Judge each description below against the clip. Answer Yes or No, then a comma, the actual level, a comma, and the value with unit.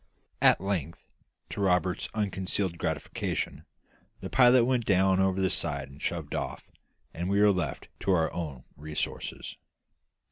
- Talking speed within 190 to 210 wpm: No, average, 140 wpm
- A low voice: Yes, very low, 95 Hz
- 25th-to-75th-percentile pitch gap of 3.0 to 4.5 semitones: Yes, average, 3.3 semitones